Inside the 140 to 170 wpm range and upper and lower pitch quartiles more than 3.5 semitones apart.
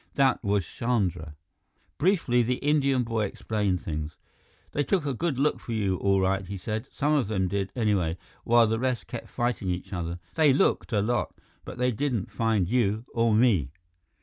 No: average, 180 wpm; average, 4.6 semitones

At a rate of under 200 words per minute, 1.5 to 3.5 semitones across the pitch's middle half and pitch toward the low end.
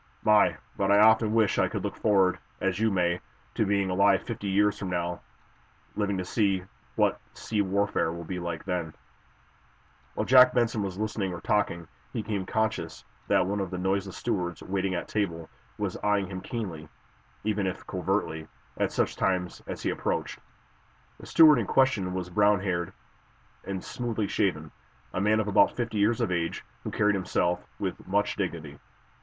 Yes: average, 170 wpm; average, 2.7 semitones; low, 100 Hz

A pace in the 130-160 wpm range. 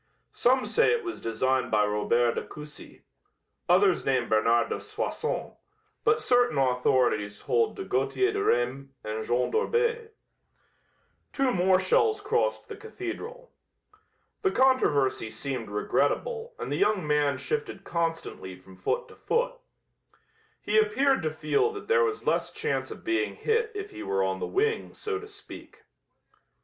Yes: average, 150 wpm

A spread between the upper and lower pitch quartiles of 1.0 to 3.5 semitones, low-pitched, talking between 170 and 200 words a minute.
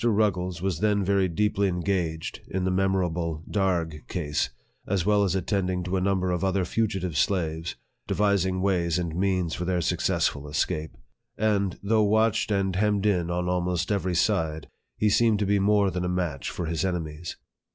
Yes: average, 2.7 semitones; very low, 95 Hz; average, 180 wpm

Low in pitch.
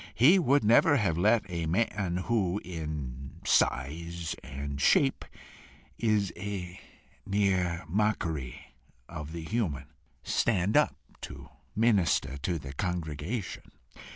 Yes: very low, 90 Hz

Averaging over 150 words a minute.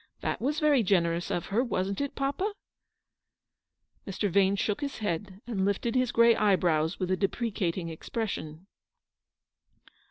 No: average, 145 wpm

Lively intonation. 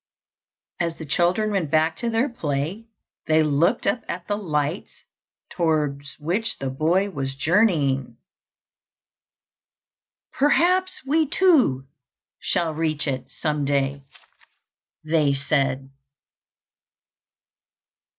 Yes: wide, 6.5 semitones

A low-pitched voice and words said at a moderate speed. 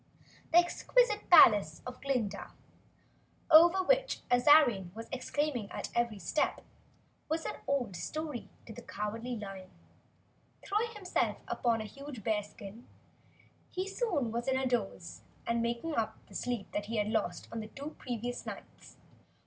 No: high, 245 Hz; average, 145 wpm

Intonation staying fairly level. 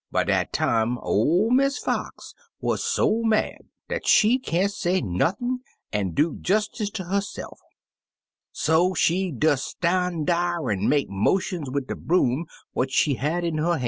No: wide, 5.6 semitones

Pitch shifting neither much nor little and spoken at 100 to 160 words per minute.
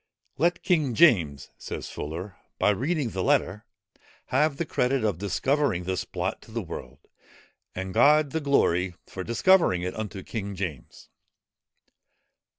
No: wide, 7.7 semitones; average, 140 wpm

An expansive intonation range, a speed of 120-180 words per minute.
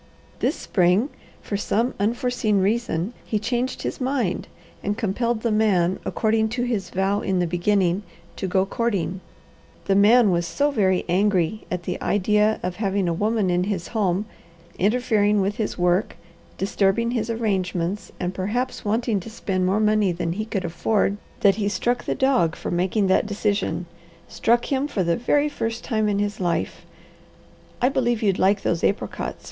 No: average, 3.4 semitones; average, 170 wpm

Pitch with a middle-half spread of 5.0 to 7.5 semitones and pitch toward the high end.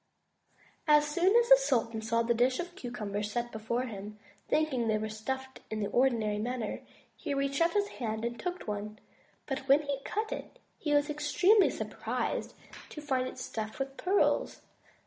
Yes: average, 5.3 semitones; very high, 255 Hz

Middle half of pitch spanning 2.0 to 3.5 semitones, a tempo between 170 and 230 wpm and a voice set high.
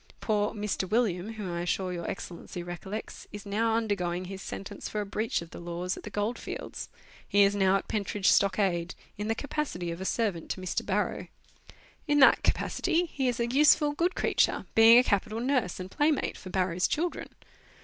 No: average, 4.0 semitones; average, 195 wpm; high, 205 Hz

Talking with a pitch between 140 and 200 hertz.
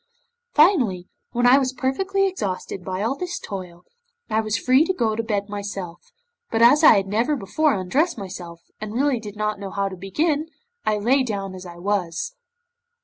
No: high, 215 Hz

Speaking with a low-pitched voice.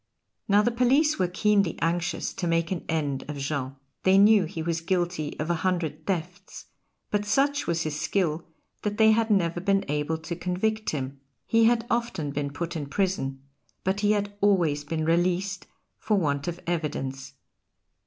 No: medium, 175 Hz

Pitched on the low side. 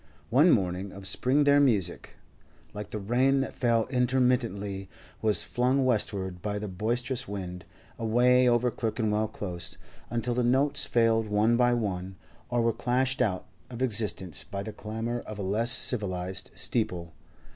Yes: low, 115 Hz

